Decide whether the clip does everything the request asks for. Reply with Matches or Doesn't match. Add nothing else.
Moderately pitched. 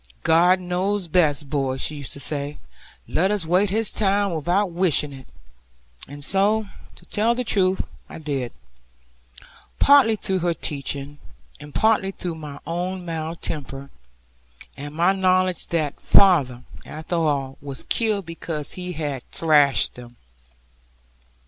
Matches